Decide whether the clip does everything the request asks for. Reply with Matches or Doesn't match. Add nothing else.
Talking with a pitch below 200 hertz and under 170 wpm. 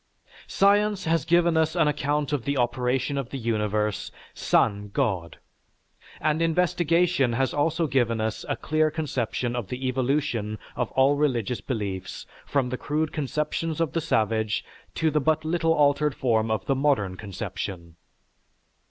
Matches